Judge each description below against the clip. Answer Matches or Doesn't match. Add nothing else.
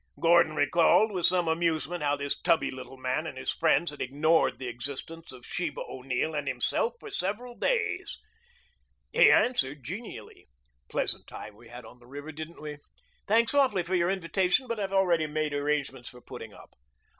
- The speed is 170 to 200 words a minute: Matches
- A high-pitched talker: Doesn't match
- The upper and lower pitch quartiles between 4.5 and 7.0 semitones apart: Matches